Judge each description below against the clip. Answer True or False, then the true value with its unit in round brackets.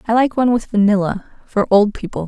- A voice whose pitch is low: False (215 Hz)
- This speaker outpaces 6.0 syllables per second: True (6.4 syllables/s)